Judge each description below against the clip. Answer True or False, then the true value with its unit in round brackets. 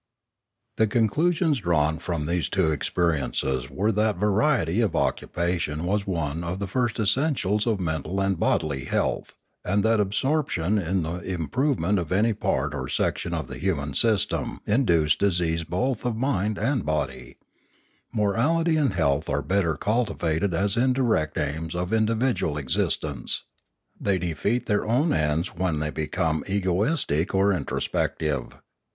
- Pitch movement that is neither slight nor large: False (5.7 semitones)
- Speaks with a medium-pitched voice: False (95 Hz)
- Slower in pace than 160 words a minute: True (145 wpm)